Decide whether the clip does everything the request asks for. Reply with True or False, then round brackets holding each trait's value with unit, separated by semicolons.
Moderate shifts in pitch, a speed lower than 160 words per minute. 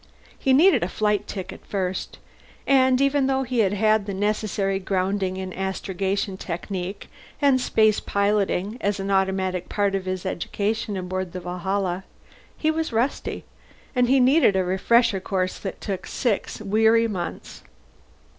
True (3.1 semitones; 140 wpm)